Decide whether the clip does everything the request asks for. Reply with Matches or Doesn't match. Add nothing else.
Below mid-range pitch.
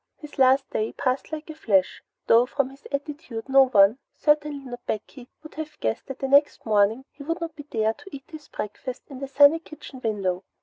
Doesn't match